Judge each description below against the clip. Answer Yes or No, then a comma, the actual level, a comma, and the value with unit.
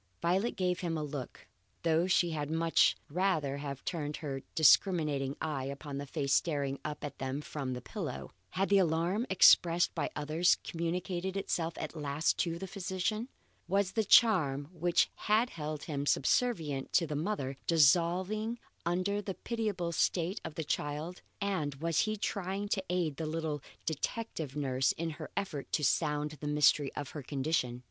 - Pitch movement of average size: Yes, average, 4.1 semitones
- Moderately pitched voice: Yes, medium, 165 Hz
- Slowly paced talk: No, average, 165 wpm